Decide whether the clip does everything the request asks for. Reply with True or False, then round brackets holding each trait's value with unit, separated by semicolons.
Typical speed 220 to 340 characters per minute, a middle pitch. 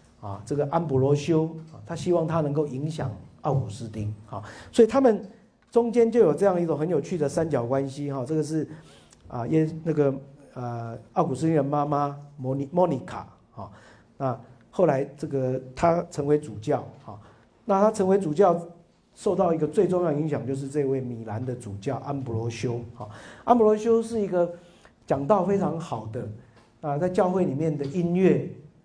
True (255 characters per minute; 145 Hz)